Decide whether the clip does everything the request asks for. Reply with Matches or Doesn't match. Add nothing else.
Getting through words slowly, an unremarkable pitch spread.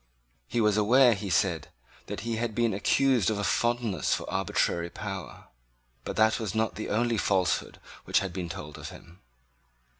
Doesn't match